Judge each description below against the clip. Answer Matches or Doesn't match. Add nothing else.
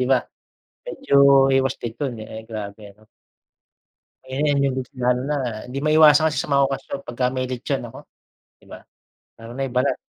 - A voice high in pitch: Doesn't match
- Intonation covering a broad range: Doesn't match